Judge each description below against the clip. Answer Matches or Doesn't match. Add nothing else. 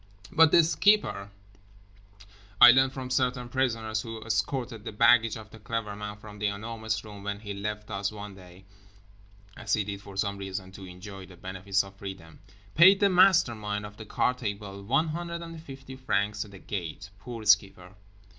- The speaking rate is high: Doesn't match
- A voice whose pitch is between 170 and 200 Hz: Doesn't match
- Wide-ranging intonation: Doesn't match